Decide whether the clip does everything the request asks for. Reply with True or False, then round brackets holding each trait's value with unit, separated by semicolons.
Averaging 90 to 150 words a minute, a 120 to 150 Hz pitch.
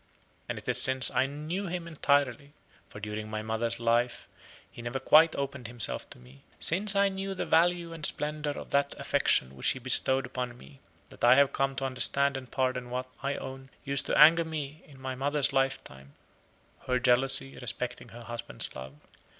False (185 wpm; 135 Hz)